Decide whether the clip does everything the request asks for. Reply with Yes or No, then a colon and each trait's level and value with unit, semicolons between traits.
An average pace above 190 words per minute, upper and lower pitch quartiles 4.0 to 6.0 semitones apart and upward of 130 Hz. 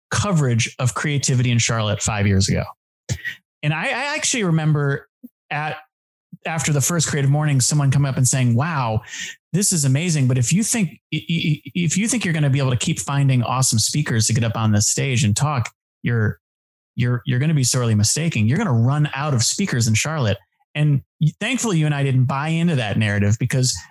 Yes: fast, 205 wpm; average, 4.7 semitones; medium, 140 Hz